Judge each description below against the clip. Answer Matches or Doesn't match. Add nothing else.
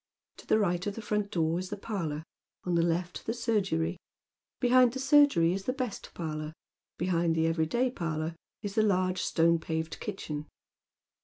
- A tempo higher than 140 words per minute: Matches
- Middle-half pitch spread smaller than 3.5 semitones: Doesn't match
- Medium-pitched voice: Matches